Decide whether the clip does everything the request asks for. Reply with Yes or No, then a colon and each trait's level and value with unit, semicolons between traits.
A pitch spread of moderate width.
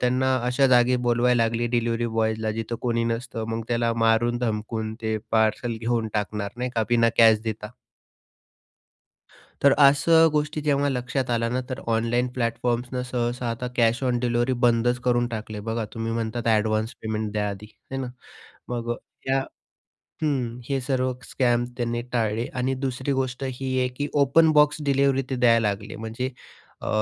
No: narrow, 2.1 semitones